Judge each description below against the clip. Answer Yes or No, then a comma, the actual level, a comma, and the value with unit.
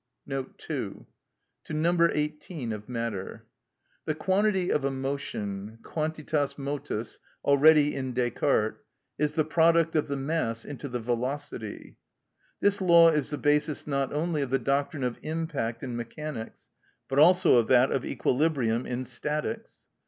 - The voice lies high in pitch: No, medium, 145 Hz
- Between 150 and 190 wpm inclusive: No, average, 140 wpm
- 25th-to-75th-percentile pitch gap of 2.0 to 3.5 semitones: No, average, 4.0 semitones